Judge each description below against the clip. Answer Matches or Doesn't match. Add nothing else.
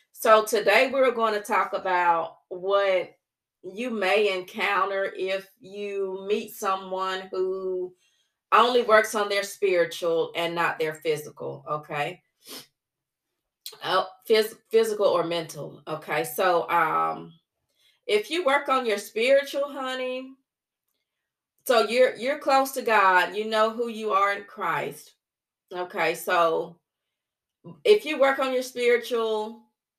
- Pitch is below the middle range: Doesn't match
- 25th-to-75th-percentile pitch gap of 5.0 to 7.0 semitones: Doesn't match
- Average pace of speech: Doesn't match